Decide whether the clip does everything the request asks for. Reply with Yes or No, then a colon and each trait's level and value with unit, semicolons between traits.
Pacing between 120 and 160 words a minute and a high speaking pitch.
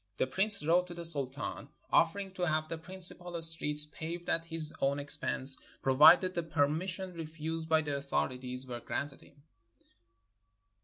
No: average, 155 wpm; medium, 160 Hz